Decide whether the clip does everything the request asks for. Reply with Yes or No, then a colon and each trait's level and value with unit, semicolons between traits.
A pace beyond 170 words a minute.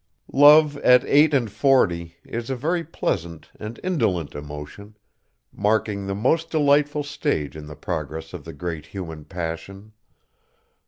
No: average, 140 wpm